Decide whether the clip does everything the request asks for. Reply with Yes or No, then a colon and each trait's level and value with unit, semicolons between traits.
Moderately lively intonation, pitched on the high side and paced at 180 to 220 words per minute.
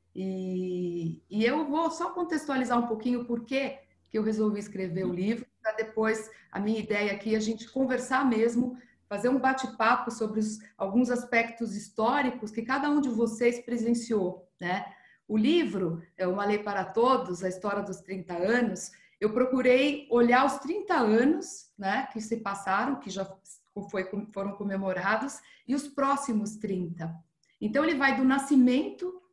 No: average, 4.7 semitones; high, 225 Hz; average, 160 wpm